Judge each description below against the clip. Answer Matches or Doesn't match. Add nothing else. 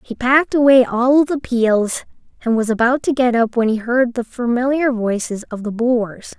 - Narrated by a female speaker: Matches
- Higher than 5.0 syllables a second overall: Doesn't match